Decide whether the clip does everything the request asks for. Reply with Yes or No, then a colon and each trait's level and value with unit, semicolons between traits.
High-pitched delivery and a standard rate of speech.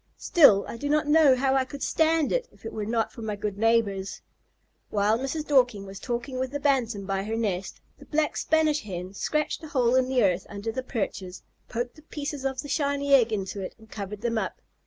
No: high, 240 Hz; fast, 220 wpm